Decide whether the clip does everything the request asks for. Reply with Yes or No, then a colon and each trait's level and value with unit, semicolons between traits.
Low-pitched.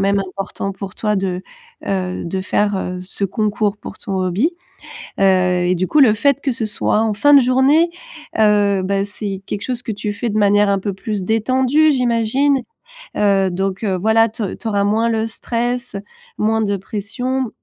No: high, 210 Hz